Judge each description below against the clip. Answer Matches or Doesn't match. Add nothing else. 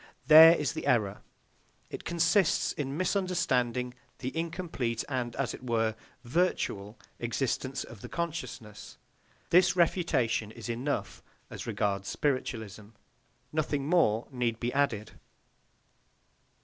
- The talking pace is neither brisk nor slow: Doesn't match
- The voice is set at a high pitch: Doesn't match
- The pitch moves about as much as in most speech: Doesn't match